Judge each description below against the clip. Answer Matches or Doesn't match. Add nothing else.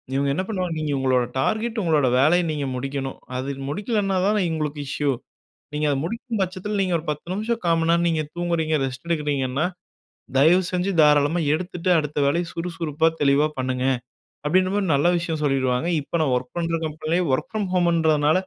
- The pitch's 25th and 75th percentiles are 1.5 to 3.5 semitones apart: Doesn't match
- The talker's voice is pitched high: Doesn't match